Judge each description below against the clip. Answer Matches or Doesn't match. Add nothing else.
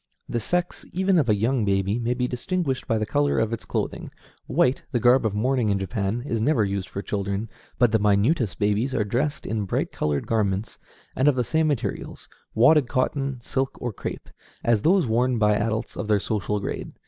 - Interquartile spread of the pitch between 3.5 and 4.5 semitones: Matches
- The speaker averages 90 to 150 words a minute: Doesn't match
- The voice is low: Matches